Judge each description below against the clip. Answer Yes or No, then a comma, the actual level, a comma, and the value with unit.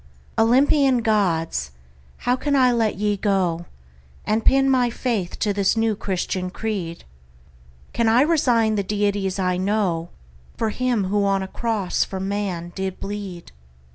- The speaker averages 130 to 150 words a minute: Yes, average, 145 wpm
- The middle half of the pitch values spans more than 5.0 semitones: No, average, 3.4 semitones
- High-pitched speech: Yes, high, 205 Hz